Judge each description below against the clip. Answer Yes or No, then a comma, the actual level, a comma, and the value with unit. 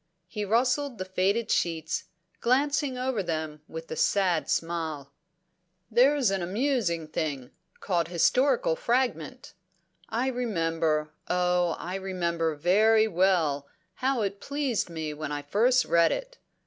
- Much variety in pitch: Yes, wide, 7.0 semitones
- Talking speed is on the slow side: Yes, slow, 125 wpm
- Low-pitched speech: No, medium, 185 Hz